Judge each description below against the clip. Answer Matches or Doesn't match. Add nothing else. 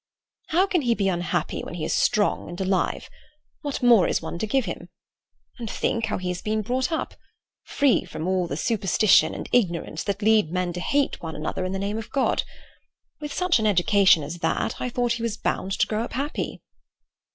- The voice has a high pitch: Matches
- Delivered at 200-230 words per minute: Matches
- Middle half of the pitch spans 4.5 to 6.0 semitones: Matches